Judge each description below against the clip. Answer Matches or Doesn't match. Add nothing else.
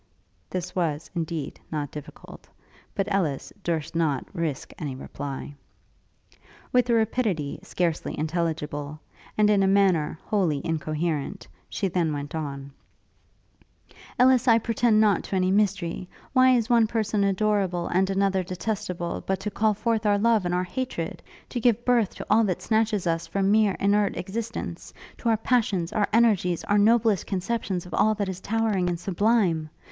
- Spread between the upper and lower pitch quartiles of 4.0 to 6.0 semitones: Matches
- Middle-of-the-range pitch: Doesn't match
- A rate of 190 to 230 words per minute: Doesn't match